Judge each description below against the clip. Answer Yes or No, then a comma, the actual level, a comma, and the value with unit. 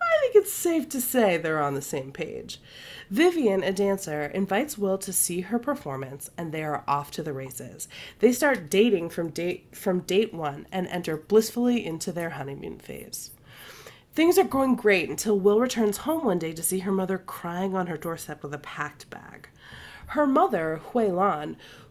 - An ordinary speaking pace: Yes, average, 185 wpm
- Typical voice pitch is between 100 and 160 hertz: No, high, 190 Hz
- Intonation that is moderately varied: No, wide, 6.1 semitones